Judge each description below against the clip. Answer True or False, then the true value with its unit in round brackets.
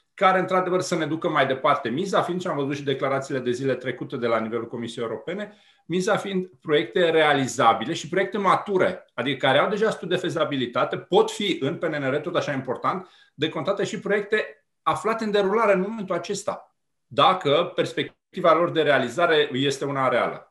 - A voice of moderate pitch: True (175 Hz)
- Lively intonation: True (5.9 semitones)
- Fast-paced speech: True (180 wpm)